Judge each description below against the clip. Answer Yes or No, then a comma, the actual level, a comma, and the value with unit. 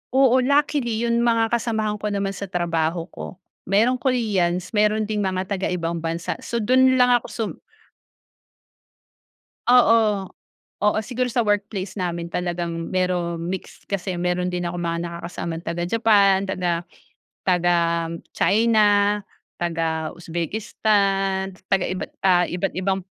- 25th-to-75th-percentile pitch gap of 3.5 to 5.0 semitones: Yes, average, 3.9 semitones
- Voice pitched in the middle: No, high, 195 Hz